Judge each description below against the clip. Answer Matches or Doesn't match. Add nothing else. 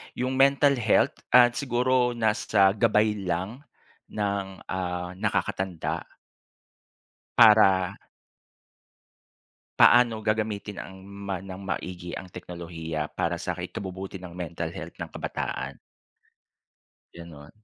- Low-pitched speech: Matches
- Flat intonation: Doesn't match